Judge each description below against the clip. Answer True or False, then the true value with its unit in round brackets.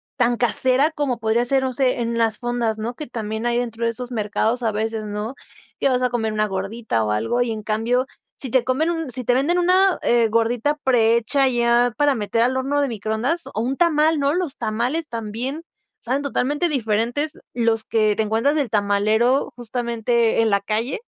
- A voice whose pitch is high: True (240 Hz)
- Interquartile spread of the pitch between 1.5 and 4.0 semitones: True (3.3 semitones)